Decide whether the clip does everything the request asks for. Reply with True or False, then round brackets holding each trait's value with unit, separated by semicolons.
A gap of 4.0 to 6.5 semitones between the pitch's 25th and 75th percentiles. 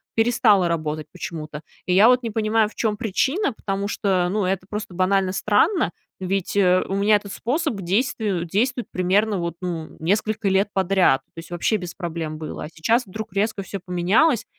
False (3.4 semitones)